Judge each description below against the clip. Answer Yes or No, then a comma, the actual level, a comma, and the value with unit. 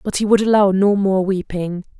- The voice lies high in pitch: Yes, high, 195 Hz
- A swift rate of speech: Yes, fast, 210 wpm